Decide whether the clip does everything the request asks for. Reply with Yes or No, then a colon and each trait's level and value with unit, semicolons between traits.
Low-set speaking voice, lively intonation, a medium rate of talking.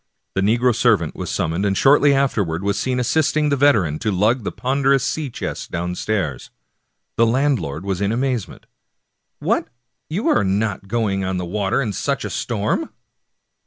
Yes: low, 110 Hz; wide, 5.7 semitones; average, 170 wpm